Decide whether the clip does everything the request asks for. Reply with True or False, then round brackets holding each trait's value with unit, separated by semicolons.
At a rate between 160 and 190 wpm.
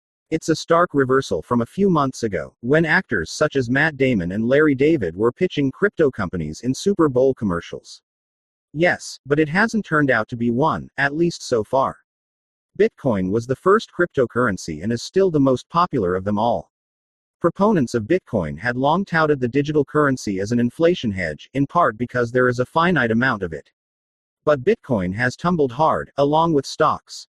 True (185 wpm)